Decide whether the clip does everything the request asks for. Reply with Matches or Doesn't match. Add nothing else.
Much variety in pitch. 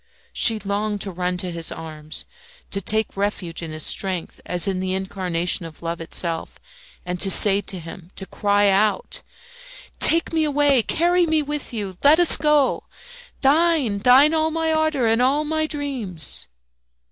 Matches